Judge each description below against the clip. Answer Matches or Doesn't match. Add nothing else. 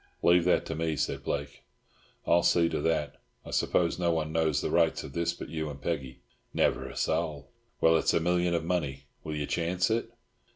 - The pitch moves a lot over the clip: Doesn't match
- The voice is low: Matches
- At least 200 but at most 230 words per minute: Matches